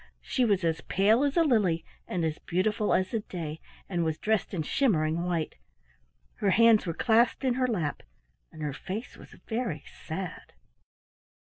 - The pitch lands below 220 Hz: Yes, high, 190 Hz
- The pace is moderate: Yes, average, 170 wpm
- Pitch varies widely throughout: Yes, wide, 5.7 semitones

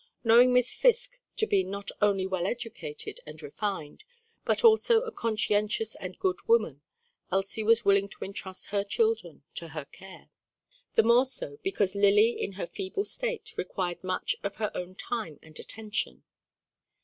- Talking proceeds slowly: No, average, 160 wpm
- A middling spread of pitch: Yes, average, 4.4 semitones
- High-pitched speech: Yes, high, 205 Hz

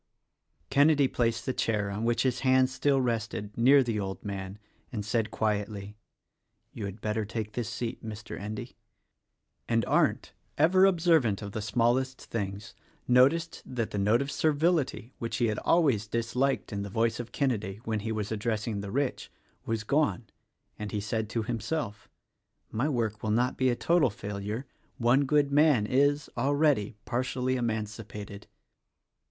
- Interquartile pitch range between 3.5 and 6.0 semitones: Yes, average, 3.9 semitones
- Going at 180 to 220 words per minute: No, average, 165 wpm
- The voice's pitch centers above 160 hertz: No, low, 115 Hz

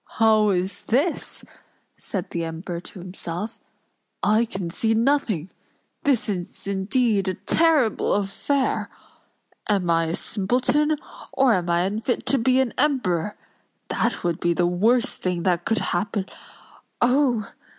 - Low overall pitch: No, high, 205 Hz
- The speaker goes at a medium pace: No, slow, 130 wpm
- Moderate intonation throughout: No, wide, 5.7 semitones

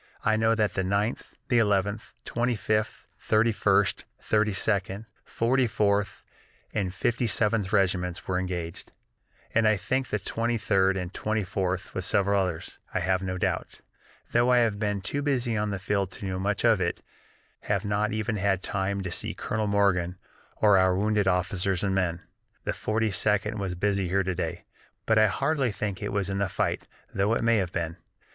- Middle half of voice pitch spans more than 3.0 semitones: No, narrow, 2.5 semitones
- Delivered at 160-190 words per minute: Yes, average, 185 wpm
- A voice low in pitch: Yes, low, 100 Hz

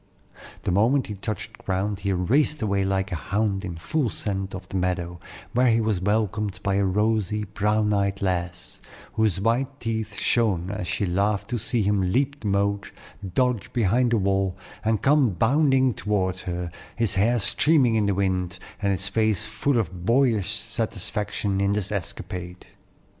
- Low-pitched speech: Yes, low, 100 Hz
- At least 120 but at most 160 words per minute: No, average, 170 wpm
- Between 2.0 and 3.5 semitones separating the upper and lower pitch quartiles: Yes, average, 2.9 semitones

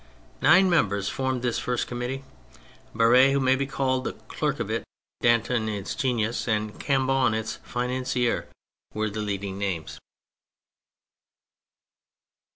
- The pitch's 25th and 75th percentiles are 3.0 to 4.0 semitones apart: Yes, average, 3.5 semitones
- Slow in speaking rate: Yes, slow, 125 wpm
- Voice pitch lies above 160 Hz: No, low, 120 Hz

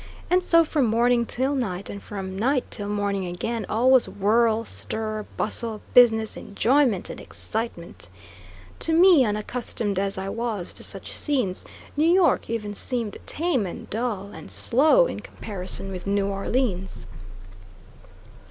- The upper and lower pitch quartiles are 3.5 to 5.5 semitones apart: Yes, average, 4.2 semitones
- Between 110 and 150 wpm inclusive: Yes, average, 145 wpm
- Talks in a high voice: Yes, high, 220 Hz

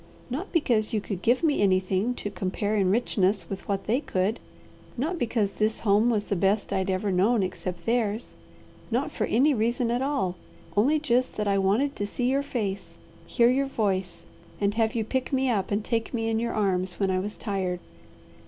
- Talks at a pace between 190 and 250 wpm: Yes, average, 200 wpm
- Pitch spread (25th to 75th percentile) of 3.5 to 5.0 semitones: Yes, average, 3.8 semitones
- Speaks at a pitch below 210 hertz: No, high, 215 Hz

